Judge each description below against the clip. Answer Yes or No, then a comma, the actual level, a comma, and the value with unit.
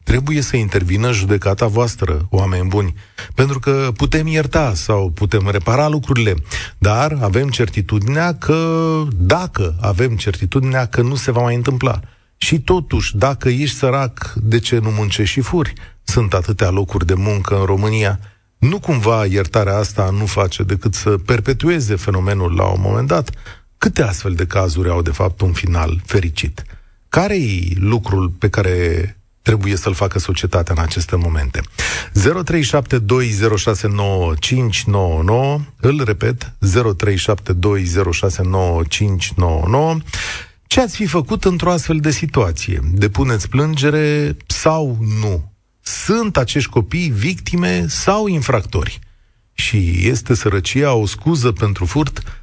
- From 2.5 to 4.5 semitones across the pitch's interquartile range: No, wide, 5.5 semitones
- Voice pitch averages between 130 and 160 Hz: No, low, 105 Hz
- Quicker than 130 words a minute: No, average, 125 wpm